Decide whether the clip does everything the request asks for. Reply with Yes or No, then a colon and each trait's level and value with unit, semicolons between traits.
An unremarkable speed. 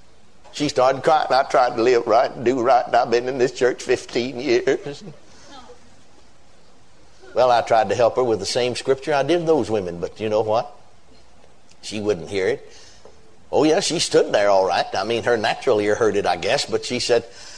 No: fast, 210 wpm